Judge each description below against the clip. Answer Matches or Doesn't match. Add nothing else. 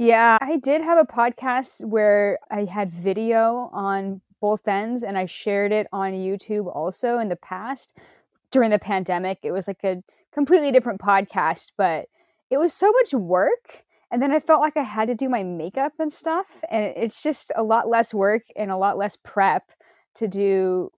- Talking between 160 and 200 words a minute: Matches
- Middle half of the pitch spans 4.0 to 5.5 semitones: Matches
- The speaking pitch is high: Matches